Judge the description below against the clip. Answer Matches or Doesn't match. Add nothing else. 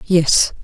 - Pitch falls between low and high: Matches